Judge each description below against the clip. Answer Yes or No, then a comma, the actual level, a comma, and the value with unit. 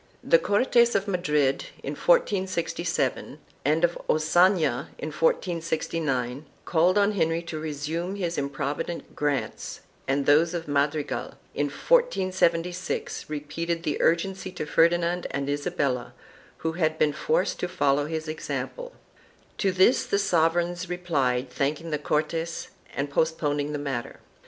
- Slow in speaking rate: Yes, slow, 130 wpm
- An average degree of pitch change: Yes, average, 3.5 semitones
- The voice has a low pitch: No, medium, 165 Hz